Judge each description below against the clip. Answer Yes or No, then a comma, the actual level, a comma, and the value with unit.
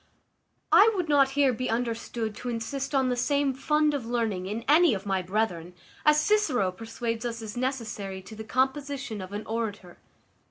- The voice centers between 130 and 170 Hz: No, high, 235 Hz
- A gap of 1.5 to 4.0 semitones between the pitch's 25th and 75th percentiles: No, average, 4.4 semitones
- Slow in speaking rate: No, average, 175 wpm